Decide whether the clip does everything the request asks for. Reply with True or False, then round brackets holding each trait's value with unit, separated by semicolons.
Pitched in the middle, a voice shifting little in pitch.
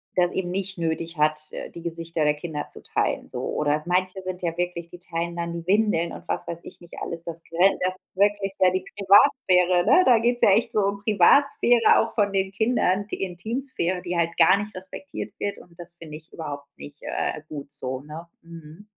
False (180 Hz; 3.0 semitones)